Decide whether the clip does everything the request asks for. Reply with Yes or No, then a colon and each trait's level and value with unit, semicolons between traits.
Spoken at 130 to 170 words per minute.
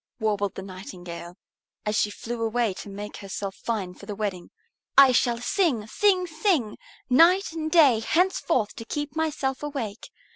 Yes: average, 155 wpm